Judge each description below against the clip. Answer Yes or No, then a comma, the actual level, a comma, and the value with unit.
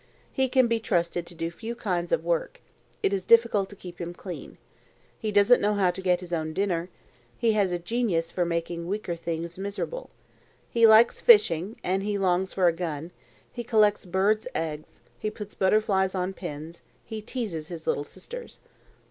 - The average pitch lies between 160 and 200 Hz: Yes, high, 190 Hz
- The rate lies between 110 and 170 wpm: No, average, 180 wpm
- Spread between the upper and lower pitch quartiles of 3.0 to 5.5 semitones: Yes, average, 4.0 semitones